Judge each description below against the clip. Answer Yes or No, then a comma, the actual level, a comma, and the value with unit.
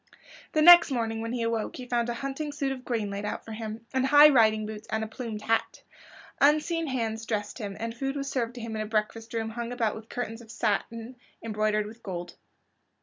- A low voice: No, high, 230 Hz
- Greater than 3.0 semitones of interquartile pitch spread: No, average, 2.7 semitones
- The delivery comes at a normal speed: No, fast, 220 wpm